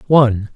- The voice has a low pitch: Yes, low, 120 Hz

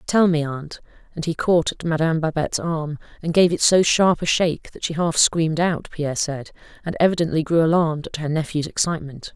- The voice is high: No, medium, 160 Hz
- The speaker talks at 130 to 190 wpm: No, fast, 205 wpm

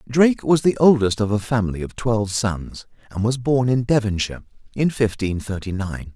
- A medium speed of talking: Yes, average, 185 wpm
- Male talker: Yes, male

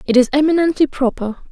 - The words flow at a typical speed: Yes, average, 160 wpm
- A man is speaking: No, female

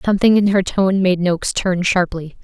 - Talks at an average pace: Yes, average, 195 wpm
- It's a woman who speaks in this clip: Yes, female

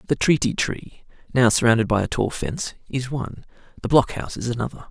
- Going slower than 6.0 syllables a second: No, 6.2 syllables/s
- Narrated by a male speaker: Yes, male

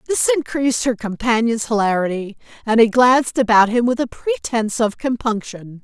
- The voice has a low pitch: No, high, 235 Hz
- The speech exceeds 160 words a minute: No, average, 155 wpm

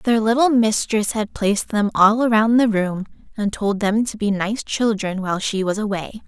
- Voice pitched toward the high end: Yes, high, 210 Hz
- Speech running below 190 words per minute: No, average, 200 wpm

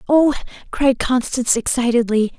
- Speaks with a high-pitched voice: Yes, very high, 250 Hz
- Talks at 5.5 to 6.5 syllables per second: No, 5.0 syllables/s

